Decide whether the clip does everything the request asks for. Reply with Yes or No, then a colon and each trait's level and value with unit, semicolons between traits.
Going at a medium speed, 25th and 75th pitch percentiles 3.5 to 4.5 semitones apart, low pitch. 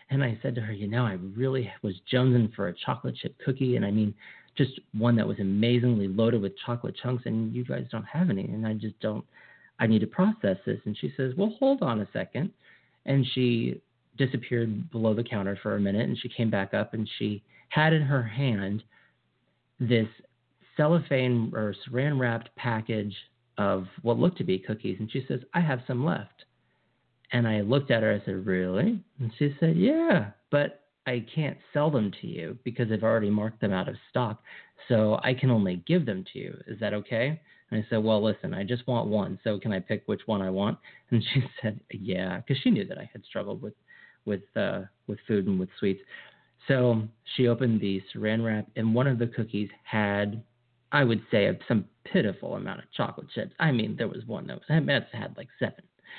No: fast, 210 wpm; average, 3.8 semitones; low, 115 Hz